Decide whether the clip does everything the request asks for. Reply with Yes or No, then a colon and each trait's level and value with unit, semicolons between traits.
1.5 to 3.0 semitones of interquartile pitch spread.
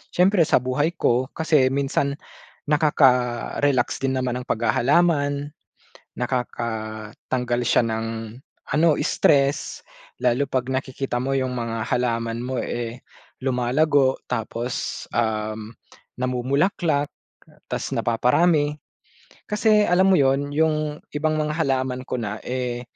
No: average, 3.4 semitones